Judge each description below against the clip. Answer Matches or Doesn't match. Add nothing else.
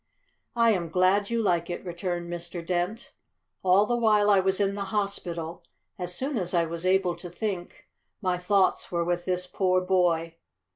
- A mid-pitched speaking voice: Matches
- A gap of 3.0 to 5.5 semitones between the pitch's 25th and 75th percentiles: Doesn't match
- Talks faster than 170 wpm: Matches